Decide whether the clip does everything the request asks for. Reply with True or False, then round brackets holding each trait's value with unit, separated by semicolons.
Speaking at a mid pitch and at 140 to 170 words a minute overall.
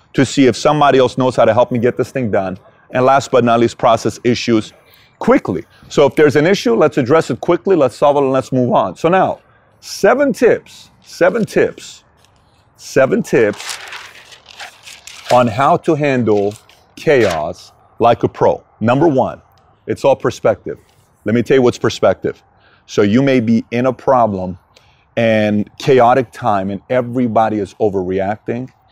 False (125 Hz; 165 wpm)